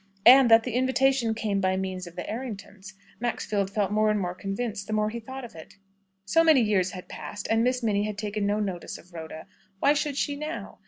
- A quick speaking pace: Yes, fast, 220 wpm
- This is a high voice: Yes, high, 215 Hz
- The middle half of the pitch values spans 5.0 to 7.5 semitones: No, average, 3.9 semitones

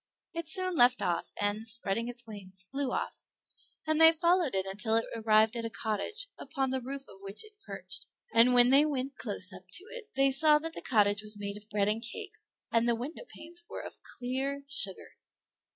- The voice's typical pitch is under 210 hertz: No, high, 245 Hz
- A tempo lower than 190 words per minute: No, average, 200 wpm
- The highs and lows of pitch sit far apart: Yes, wide, 6.1 semitones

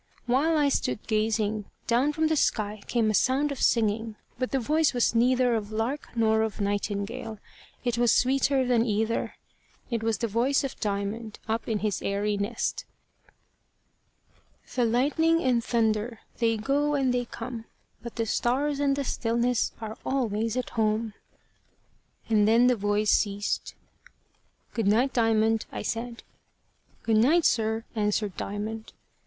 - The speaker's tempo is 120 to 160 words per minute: Yes, average, 150 wpm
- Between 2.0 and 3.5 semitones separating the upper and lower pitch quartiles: Yes, average, 2.8 semitones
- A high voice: Yes, high, 230 Hz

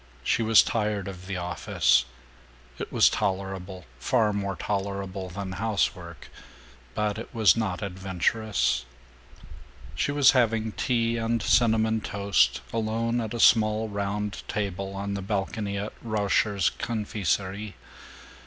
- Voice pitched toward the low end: Yes, low, 100 Hz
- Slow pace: Yes, slow, 125 wpm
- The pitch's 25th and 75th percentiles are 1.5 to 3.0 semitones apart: Yes, narrow, 2.4 semitones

